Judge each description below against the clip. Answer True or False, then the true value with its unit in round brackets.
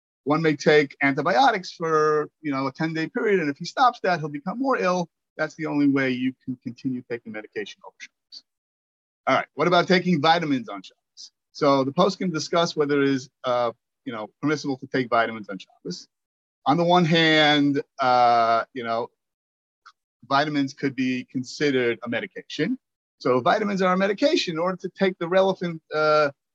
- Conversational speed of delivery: True (185 wpm)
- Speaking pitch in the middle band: True (145 Hz)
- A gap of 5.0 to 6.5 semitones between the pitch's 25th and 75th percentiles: True (5.3 semitones)